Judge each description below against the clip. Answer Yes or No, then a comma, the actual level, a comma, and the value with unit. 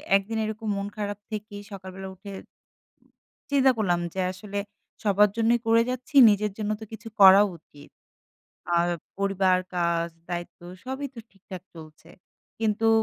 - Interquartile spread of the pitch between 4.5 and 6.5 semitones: No, average, 2.9 semitones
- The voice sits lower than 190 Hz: No, high, 200 Hz